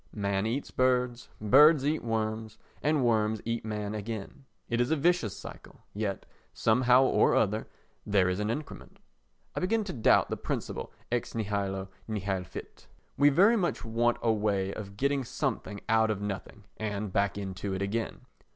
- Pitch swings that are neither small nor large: Yes, average, 3.7 semitones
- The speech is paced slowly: No, average, 165 wpm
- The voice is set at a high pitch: No, low, 110 Hz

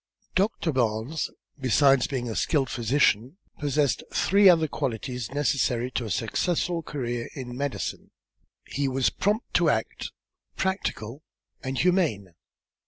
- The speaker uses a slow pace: Yes, slow, 120 wpm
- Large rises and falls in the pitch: No, average, 4.7 semitones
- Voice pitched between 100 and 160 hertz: Yes, low, 135 Hz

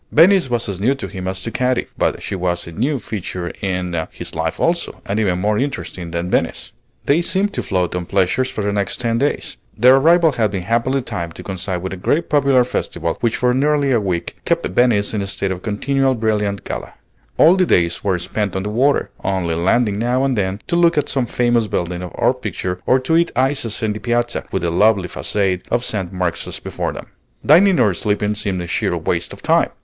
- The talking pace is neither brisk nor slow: No, fast, 220 wpm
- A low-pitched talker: Yes, low, 105 Hz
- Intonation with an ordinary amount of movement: No, wide, 5.8 semitones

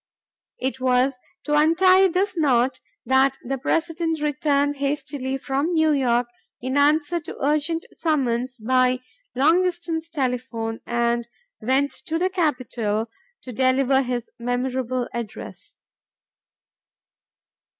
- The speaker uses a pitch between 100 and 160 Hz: No, very high, 270 Hz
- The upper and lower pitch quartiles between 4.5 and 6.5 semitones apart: No, average, 3.9 semitones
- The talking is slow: Yes, slow, 110 wpm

